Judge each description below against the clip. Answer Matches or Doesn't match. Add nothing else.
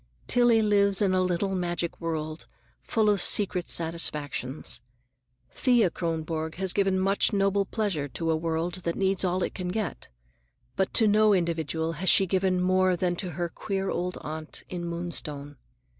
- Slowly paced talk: Doesn't match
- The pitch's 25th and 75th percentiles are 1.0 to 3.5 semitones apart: Matches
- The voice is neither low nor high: Matches